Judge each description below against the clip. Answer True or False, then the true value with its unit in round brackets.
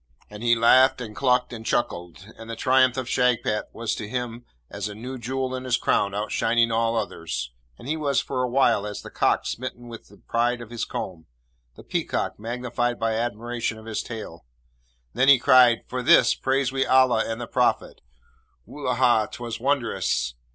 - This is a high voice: False (120 Hz)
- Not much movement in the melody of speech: True (2.3 semitones)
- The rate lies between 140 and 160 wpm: False (180 wpm)